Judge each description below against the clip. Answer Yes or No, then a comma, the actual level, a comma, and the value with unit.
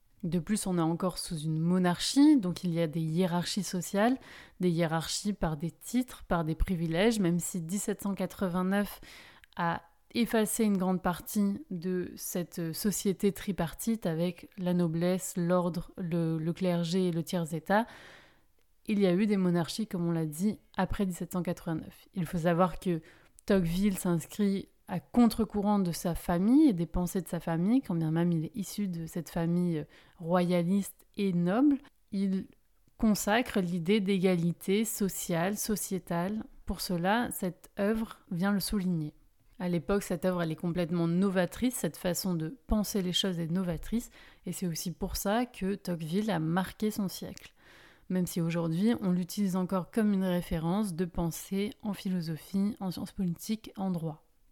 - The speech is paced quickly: No, average, 160 wpm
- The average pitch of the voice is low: No, medium, 185 Hz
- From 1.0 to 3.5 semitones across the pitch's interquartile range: Yes, average, 2.8 semitones